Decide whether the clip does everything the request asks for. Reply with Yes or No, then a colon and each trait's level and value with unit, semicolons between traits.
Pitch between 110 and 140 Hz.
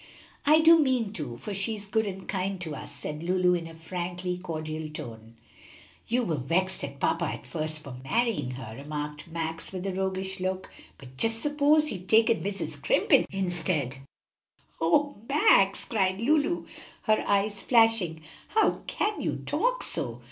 No: medium, 185 Hz